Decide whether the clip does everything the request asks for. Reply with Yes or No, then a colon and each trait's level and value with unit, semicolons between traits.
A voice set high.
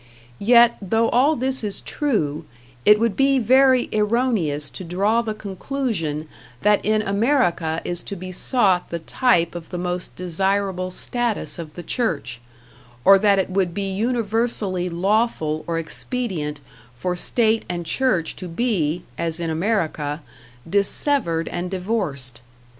Yes: high, 195 Hz